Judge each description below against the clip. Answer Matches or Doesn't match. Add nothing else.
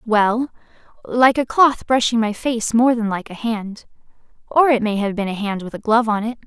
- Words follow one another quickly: Matches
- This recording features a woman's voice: Matches